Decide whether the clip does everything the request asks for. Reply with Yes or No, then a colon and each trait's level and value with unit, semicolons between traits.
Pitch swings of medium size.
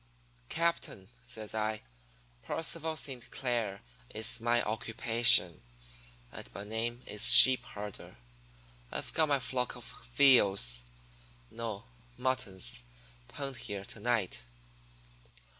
Yes: average, 4.0 semitones